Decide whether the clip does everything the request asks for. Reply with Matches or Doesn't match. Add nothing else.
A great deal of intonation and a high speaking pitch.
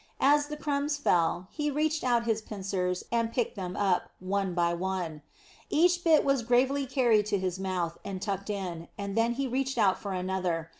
Matches